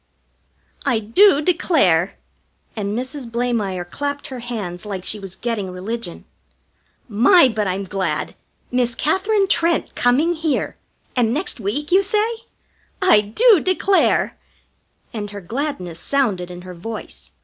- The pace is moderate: No, slow, 130 wpm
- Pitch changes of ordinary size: No, wide, 7.3 semitones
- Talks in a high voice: Yes, high, 235 Hz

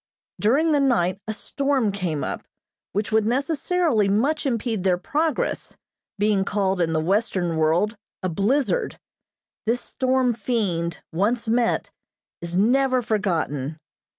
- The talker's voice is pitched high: Yes, high, 215 Hz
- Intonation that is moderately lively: No, wide, 5.7 semitones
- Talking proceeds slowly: Yes, slow, 125 wpm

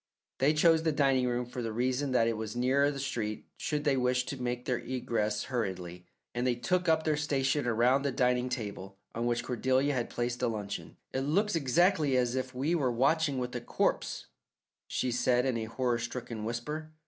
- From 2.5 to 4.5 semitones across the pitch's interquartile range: Yes, average, 2.8 semitones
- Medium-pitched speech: No, low, 125 Hz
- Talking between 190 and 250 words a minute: Yes, average, 200 wpm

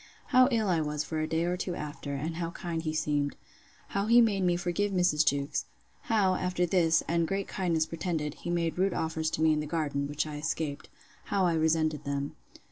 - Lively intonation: No, average, 3.0 semitones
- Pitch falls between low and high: Yes, medium, 165 Hz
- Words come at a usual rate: No, fast, 210 wpm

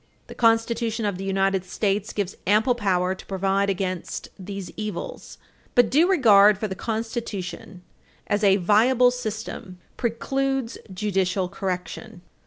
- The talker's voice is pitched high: Yes, high, 205 Hz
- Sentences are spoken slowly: Yes, slow, 130 wpm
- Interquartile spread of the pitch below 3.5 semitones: Yes, average, 3.1 semitones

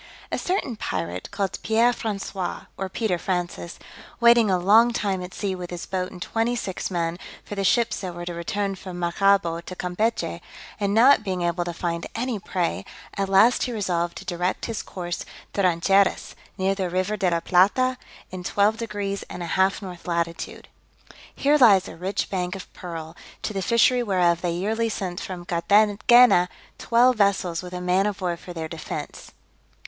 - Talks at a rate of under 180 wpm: No, average, 185 wpm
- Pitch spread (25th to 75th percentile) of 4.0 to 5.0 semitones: No, average, 3.2 semitones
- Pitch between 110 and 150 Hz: No, high, 190 Hz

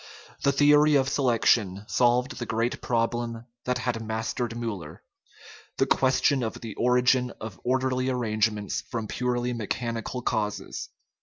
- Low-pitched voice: Yes, low, 120 Hz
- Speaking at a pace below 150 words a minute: Yes, slow, 135 wpm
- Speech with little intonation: Yes, narrow, 2.3 semitones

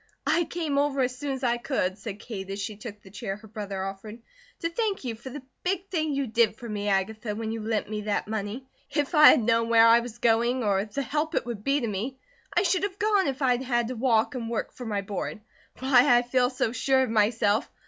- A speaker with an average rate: No, fast, 245 wpm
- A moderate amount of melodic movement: Yes, average, 4.2 semitones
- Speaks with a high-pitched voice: Yes, high, 235 Hz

